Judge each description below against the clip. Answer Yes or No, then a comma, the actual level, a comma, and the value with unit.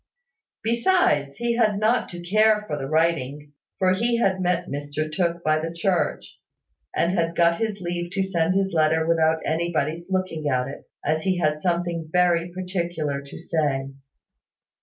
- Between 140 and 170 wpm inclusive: Yes, average, 160 wpm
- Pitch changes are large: No, average, 3.2 semitones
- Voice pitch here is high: No, medium, 170 Hz